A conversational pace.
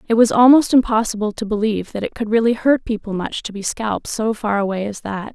No: fast, 235 wpm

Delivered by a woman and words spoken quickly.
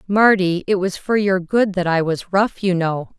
Yes: female; fast, 225 wpm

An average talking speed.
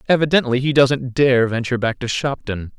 Yes: average, 170 wpm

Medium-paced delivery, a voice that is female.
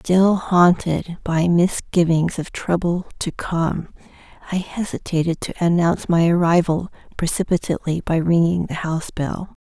No: slow, 125 wpm; female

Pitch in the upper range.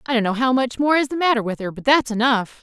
Yes: high, 245 Hz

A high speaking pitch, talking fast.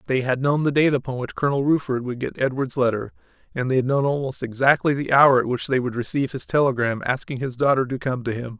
No: low, 130 Hz; fast, 245 wpm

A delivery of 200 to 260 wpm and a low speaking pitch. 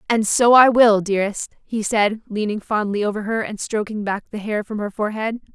No: fast, 205 wpm; high, 215 Hz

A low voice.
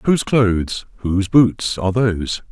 Yes: low, 105 Hz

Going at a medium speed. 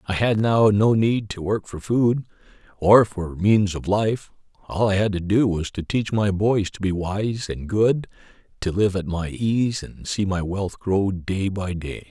No: fast, 210 wpm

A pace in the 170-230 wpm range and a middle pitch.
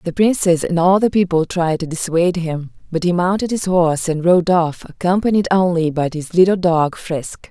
Yes: average, 200 wpm; medium, 175 Hz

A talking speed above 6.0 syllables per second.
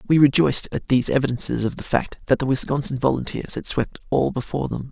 Yes: 6.4 syllables/s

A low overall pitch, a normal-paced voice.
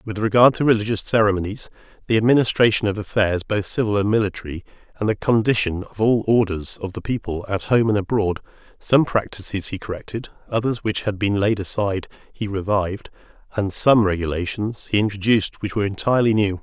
Yes: low, 105 Hz; average, 170 wpm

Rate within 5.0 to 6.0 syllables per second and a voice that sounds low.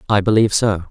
No: 7.4 syllables/s; low, 105 Hz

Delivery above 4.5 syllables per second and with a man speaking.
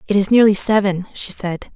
No: 5.4 syllables/s; female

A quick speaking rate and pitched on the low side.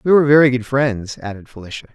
Yes: fast, 215 wpm; low, 125 Hz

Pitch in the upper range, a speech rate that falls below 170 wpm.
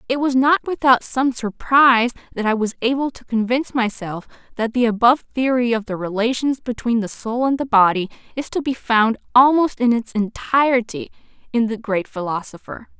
No: high, 240 Hz; average, 175 wpm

